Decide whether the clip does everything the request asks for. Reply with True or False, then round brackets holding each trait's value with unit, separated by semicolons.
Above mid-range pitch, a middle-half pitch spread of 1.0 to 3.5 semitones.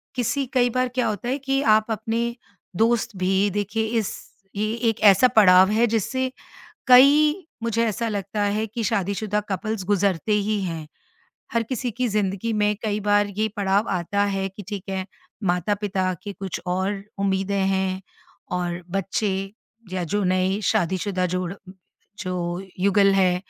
True (205 Hz; 2.8 semitones)